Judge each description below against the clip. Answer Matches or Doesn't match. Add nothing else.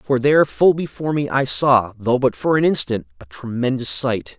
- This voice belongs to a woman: Doesn't match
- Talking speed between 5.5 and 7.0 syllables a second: Doesn't match